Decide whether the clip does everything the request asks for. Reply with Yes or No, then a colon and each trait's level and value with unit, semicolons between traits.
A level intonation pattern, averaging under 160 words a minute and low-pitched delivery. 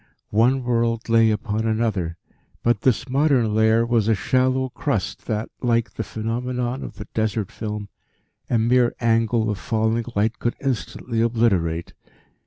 Yes: narrow, 1.8 semitones; average, 145 wpm; low, 115 Hz